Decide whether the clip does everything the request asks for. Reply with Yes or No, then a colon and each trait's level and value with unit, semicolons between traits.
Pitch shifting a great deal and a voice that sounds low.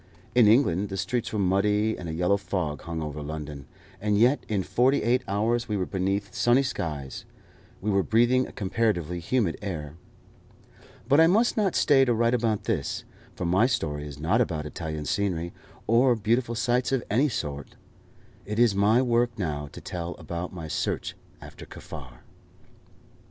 Yes: wide, 6.1 semitones; low, 100 Hz